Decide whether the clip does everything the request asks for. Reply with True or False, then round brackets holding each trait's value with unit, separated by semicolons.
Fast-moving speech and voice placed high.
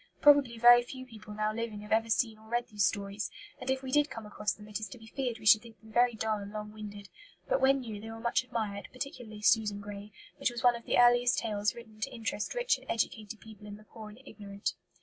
True (250 wpm; 220 Hz)